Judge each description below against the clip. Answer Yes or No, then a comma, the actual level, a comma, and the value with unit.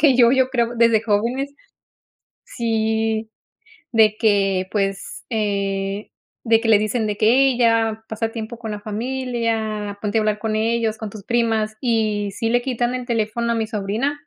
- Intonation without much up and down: Yes, narrow, 1.8 semitones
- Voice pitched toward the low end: No, high, 225 Hz